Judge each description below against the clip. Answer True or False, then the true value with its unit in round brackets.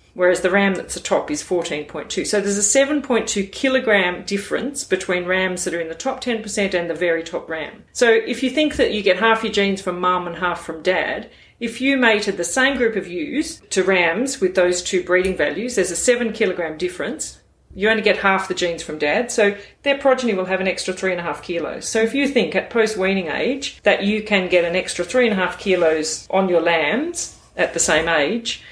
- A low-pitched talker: False (195 Hz)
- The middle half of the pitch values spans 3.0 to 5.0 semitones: True (4.5 semitones)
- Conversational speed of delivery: False (215 wpm)